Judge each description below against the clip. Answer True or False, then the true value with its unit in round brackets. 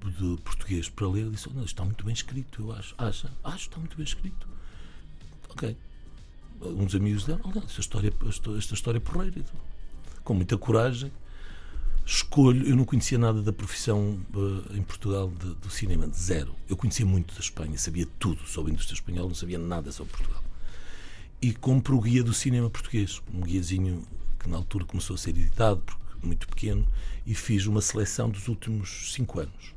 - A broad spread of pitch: False (4.5 semitones)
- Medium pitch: False (100 Hz)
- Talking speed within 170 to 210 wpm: True (185 wpm)